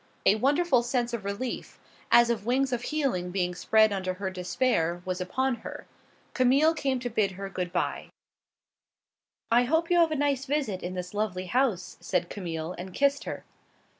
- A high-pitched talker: Yes, high, 220 Hz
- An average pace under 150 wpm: No, average, 175 wpm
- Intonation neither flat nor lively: No, wide, 6.3 semitones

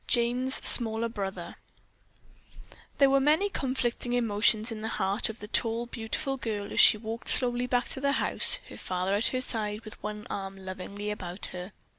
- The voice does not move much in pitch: No, average, 3.2 semitones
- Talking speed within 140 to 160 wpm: No, average, 175 wpm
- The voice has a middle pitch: No, high, 225 Hz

